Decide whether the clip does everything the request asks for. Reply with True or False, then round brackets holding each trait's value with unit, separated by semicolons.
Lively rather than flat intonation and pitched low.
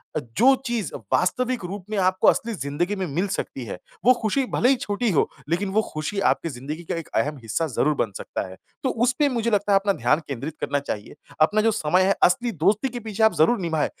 False (6.6 semitones; 190 Hz)